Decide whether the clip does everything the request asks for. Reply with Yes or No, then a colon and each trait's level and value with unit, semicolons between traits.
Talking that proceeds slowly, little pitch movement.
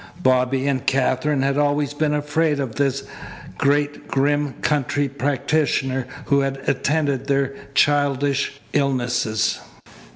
Yes: slow, 110 wpm; narrow, 1.5 semitones